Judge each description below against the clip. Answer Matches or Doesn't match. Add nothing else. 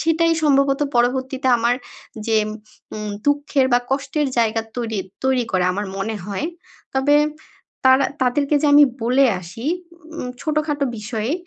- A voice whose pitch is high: Matches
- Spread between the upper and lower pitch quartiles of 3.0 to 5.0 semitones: Matches